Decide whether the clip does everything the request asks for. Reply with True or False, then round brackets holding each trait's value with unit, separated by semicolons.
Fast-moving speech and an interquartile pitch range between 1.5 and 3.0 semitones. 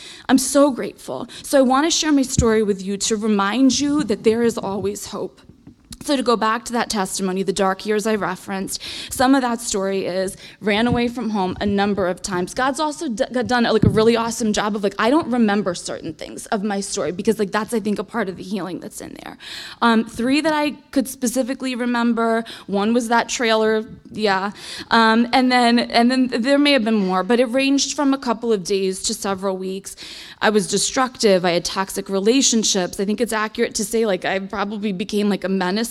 False (220 wpm; 3.7 semitones)